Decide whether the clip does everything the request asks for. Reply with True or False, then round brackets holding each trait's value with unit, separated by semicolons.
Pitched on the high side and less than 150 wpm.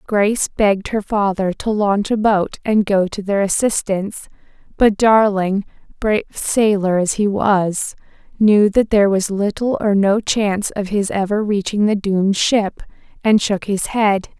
False (205 Hz; 165 wpm)